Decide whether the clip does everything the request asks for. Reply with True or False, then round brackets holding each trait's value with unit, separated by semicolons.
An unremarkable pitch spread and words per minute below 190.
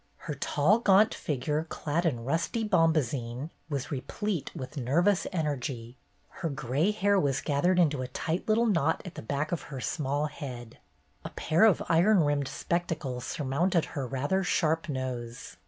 True (4.6 semitones; 160 wpm)